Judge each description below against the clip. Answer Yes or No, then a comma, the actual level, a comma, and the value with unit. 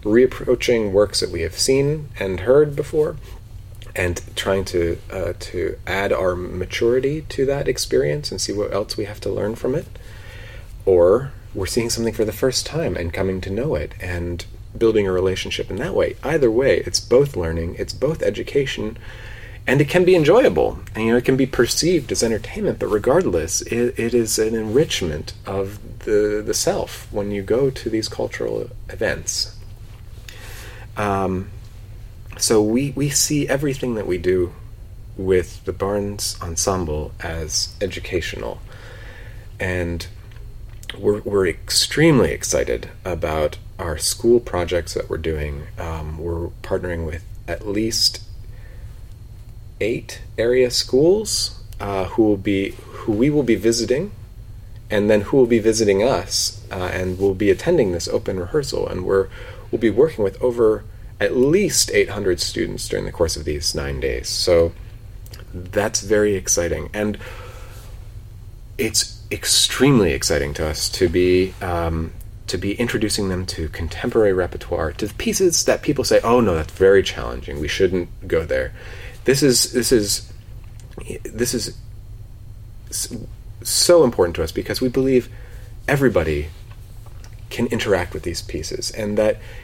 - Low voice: Yes, low, 105 Hz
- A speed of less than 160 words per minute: Yes, average, 150 wpm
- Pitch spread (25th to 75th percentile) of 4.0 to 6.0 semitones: No, average, 2.8 semitones